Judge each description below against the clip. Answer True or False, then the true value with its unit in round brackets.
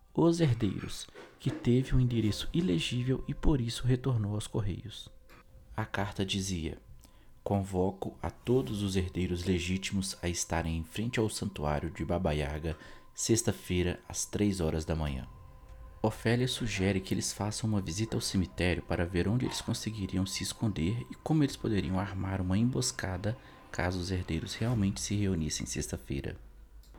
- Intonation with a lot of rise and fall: False (4.3 semitones)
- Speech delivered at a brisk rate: False (150 wpm)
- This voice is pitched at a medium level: False (95 Hz)